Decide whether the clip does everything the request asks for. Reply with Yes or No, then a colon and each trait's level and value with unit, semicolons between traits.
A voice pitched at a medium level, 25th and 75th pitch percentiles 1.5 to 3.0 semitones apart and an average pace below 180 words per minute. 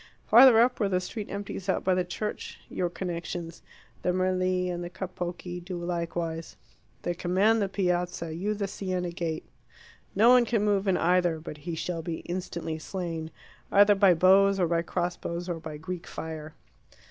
Yes: medium, 180 Hz; narrow, 2.4 semitones; average, 170 wpm